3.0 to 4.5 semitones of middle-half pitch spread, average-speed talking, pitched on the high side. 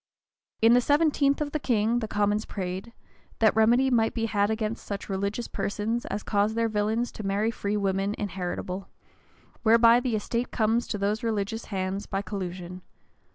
No: narrow, 2.6 semitones; average, 170 wpm; high, 215 Hz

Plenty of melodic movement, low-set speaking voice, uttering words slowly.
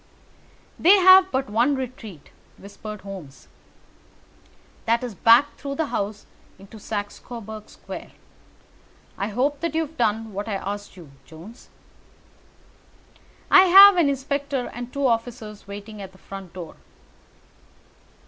No: wide, 5.7 semitones; high, 225 Hz; slow, 130 wpm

